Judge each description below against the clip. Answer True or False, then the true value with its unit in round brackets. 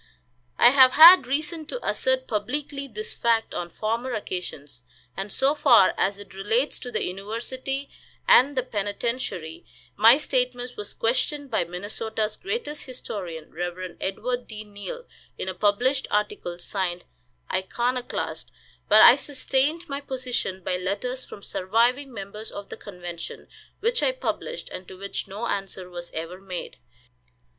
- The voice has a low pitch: False (225 Hz)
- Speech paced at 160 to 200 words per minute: False (145 wpm)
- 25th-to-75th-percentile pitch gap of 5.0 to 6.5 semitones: True (5.5 semitones)